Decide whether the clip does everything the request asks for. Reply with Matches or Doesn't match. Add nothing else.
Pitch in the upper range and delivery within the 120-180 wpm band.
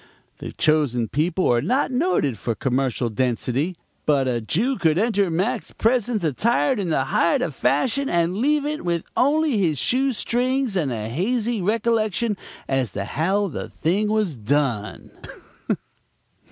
Doesn't match